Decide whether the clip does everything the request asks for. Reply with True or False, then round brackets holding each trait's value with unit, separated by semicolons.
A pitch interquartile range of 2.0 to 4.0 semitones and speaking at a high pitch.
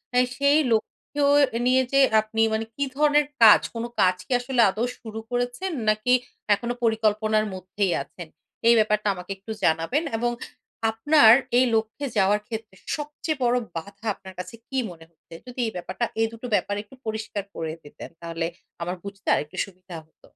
False (4.4 semitones; 220 Hz)